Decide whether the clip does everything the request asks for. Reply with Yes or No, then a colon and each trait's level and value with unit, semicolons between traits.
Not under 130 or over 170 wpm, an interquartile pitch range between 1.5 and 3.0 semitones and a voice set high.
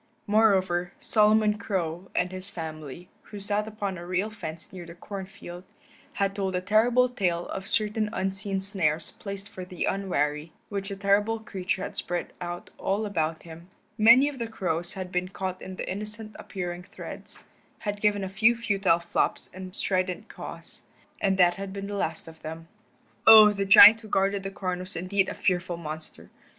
No: average, 180 wpm; narrow, 2.6 semitones; high, 195 Hz